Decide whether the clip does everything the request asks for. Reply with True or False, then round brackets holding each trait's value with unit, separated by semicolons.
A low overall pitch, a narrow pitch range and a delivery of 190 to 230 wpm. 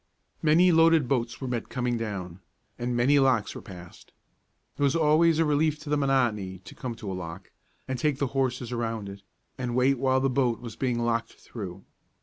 False (125 Hz; 3.7 semitones; 195 wpm)